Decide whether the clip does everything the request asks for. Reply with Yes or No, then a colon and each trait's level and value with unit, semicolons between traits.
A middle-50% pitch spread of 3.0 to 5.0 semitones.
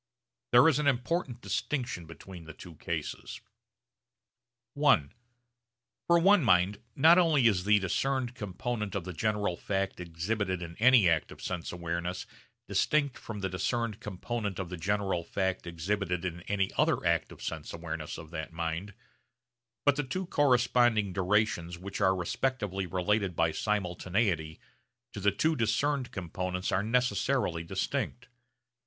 No: wide, 5.5 semitones